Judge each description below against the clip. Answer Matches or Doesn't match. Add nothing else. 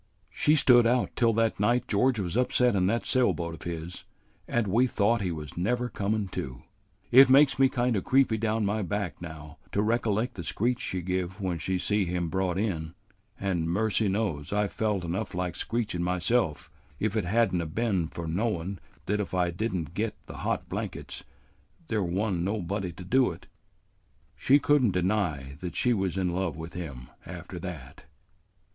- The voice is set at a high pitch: Doesn't match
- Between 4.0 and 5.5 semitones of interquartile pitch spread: Matches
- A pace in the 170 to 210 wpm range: Matches